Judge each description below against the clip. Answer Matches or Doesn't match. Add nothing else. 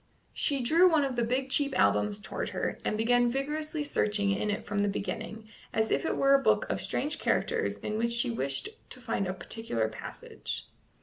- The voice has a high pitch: Matches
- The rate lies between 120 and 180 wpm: Doesn't match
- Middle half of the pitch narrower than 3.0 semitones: Doesn't match